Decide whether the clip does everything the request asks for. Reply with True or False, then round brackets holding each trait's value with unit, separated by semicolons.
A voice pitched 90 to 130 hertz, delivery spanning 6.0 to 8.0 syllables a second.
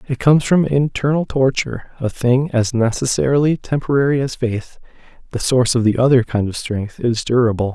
False (125 Hz; 4.5 syllables/s)